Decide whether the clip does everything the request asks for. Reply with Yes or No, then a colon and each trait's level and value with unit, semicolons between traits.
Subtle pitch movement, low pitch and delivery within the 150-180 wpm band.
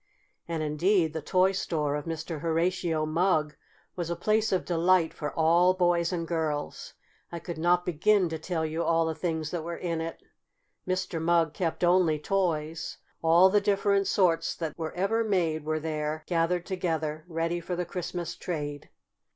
No: narrow, 2.2 semitones; medium, 170 Hz; average, 170 wpm